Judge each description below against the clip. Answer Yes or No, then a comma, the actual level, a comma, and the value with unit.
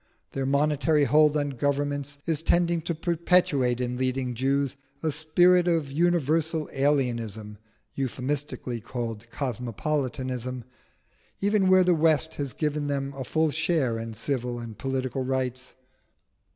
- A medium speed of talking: No, slow, 125 wpm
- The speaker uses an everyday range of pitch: Yes, average, 3.8 semitones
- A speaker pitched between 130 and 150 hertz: Yes, medium, 140 Hz